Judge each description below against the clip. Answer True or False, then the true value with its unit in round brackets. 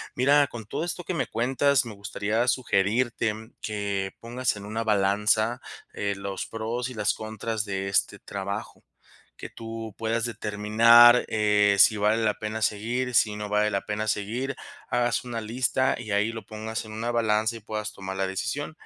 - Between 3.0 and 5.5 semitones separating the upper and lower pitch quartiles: False (2.4 semitones)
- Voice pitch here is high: False (110 Hz)